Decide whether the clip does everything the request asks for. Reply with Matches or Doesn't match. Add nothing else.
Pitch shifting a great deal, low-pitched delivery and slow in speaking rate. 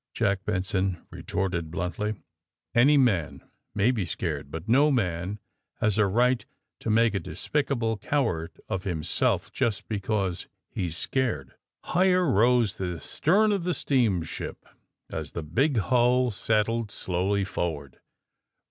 Matches